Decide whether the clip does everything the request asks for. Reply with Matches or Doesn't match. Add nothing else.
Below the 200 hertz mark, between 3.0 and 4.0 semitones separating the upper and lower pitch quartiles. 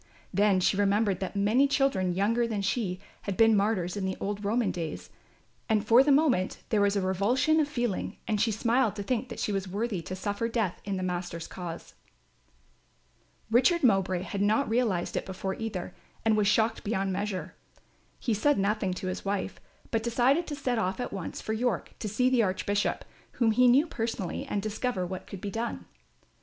Doesn't match